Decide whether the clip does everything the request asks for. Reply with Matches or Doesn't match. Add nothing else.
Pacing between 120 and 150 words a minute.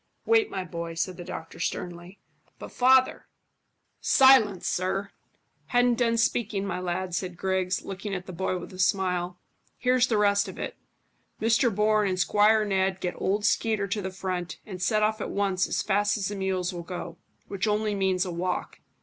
Doesn't match